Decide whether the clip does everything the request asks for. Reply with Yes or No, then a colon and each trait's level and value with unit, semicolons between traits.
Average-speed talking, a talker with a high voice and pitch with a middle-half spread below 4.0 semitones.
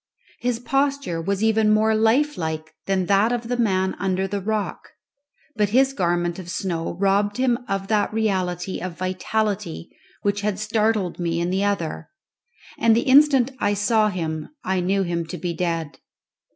Yes: average, 165 wpm; high, 200 Hz; average, 3.6 semitones